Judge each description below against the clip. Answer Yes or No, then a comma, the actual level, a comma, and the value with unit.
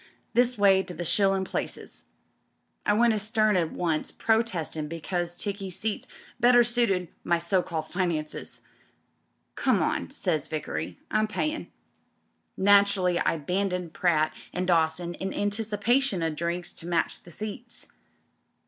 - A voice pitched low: No, medium, 185 Hz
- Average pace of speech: No, slow, 130 wpm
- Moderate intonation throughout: Yes, average, 3.9 semitones